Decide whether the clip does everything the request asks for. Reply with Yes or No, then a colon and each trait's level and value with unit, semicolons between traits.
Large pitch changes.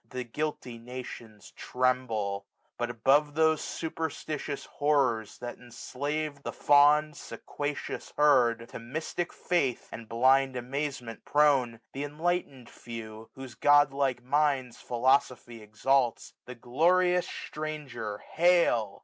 No: average, 3.7 semitones